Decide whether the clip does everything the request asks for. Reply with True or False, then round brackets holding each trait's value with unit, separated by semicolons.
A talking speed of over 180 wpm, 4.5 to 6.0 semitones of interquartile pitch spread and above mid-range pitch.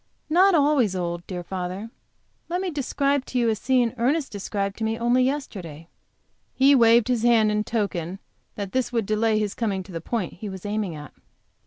True (190 wpm; 4.8 semitones; 220 Hz)